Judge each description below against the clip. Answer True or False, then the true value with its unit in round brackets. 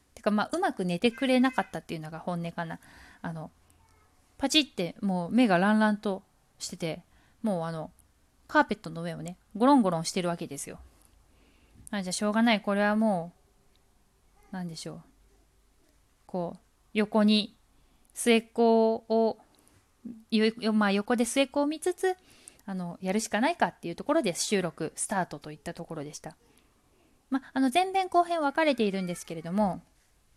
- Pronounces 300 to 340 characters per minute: False (290 characters per minute)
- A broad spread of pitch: True (5.7 semitones)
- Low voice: False (205 Hz)